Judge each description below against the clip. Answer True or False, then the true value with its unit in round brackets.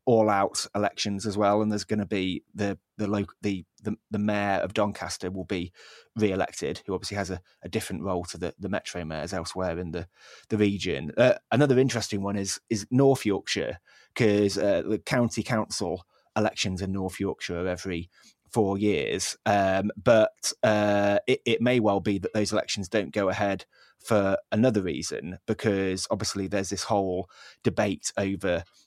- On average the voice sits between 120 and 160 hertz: False (100 Hz)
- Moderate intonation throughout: False (2.0 semitones)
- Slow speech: False (180 wpm)